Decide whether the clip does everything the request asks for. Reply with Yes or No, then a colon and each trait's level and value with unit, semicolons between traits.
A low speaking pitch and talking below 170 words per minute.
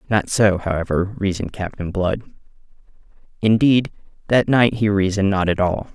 Yes: low, 100 Hz; average, 140 wpm